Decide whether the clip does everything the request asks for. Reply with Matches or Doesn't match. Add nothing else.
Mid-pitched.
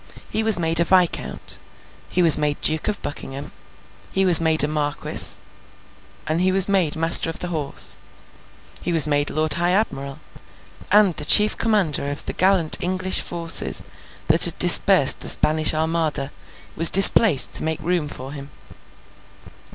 Matches